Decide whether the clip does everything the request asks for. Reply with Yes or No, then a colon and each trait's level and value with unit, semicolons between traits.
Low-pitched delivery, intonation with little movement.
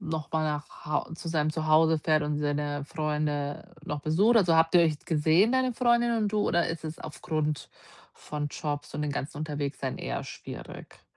No: medium, 155 Hz; narrow, 2.2 semitones